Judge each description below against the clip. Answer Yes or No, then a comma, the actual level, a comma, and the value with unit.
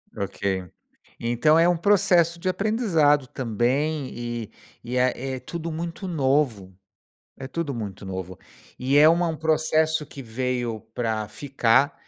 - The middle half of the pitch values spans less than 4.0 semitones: No, wide, 5.4 semitones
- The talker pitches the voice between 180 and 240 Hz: No, low, 135 Hz